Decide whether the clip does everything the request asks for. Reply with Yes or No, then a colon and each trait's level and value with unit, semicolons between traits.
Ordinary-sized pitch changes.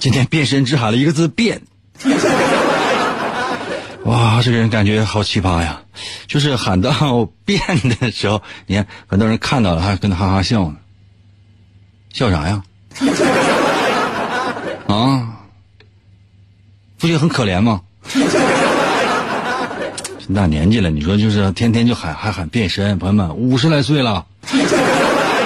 Yes: average, 3.4 semitones